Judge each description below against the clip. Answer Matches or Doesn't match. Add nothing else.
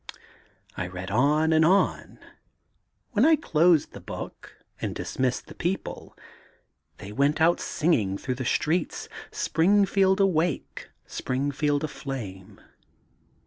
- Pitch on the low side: Doesn't match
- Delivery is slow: Matches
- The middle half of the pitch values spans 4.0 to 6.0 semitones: Matches